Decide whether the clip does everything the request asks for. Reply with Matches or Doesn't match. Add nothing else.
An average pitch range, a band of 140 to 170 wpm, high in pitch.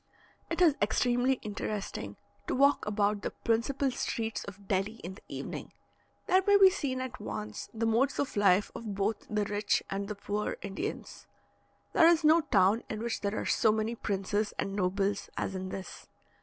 Doesn't match